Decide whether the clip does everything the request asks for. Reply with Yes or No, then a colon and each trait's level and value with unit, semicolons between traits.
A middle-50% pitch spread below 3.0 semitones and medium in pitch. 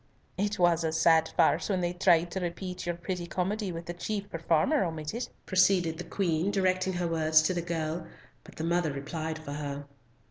Yes: narrow, 2.4 semitones; medium, 175 Hz